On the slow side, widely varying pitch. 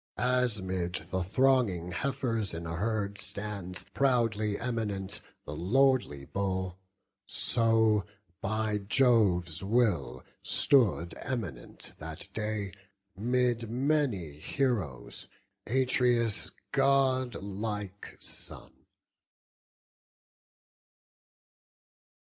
No: slow, 75 wpm; average, 4.9 semitones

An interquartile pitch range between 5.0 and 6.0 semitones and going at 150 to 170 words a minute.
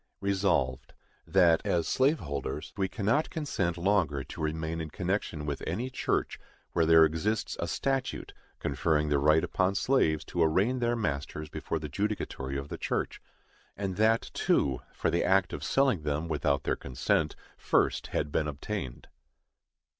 Yes: average, 5.3 semitones; average, 155 wpm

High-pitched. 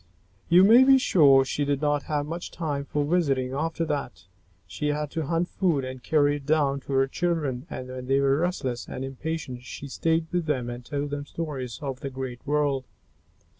No: medium, 145 Hz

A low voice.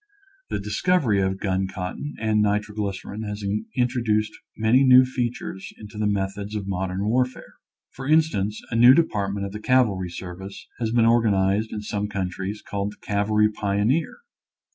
Yes: low, 105 Hz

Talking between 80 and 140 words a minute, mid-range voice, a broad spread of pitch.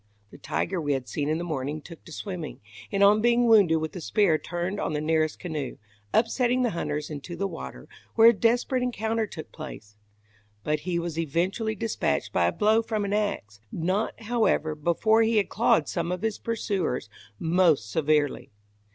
No: average, 185 wpm; medium, 180 Hz; wide, 6.0 semitones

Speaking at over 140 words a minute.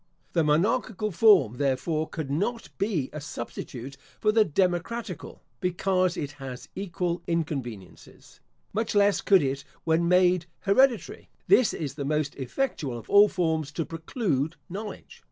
No: slow, 135 wpm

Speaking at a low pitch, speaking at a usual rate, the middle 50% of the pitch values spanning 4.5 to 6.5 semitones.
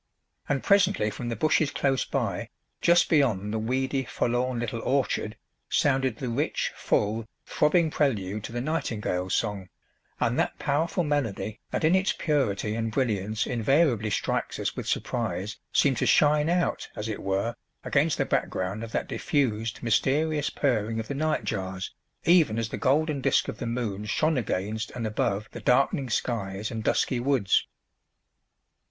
Yes: low, 120 Hz; average, 155 wpm; average, 5.0 semitones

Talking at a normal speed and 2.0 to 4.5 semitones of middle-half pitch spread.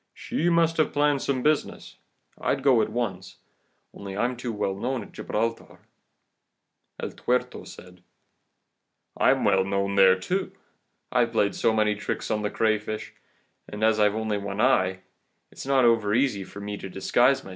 Yes: average, 165 wpm; average, 4.1 semitones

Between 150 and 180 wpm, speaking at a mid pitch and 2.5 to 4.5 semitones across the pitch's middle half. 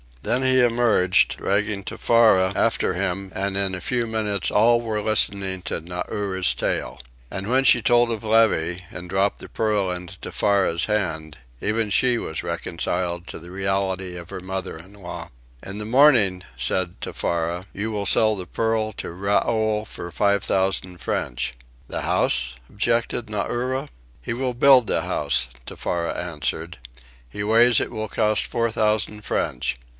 No: average, 155 wpm; low, 100 Hz; average, 3.7 semitones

